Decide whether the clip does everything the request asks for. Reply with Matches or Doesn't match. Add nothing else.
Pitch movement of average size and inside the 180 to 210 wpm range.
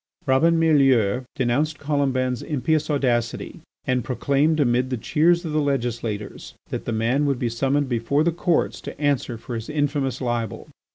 Doesn't match